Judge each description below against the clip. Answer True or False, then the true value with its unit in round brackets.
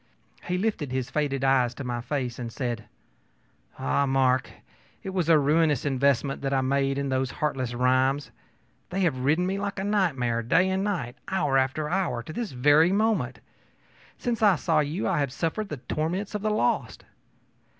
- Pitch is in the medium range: True (145 Hz)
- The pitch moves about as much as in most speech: False (5.8 semitones)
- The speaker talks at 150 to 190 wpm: True (180 wpm)